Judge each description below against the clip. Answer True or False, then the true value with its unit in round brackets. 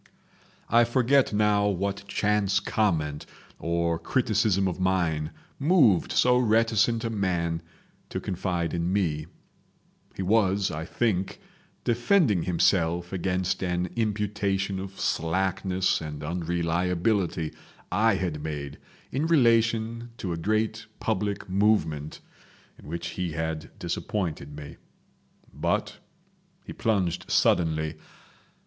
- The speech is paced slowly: True (110 wpm)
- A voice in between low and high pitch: False (95 Hz)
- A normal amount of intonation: True (4.2 semitones)